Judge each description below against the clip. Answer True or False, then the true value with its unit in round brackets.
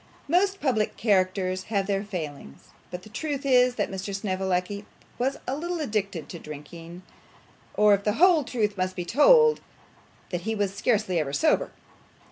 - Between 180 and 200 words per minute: False (160 wpm)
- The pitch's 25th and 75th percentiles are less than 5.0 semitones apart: False (5.4 semitones)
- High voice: True (205 Hz)